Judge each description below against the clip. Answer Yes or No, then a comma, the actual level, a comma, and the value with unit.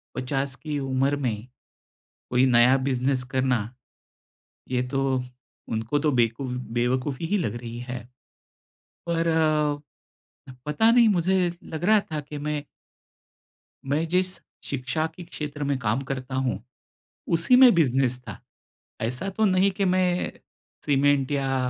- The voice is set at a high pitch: No, medium, 140 Hz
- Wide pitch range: No, average, 4.2 semitones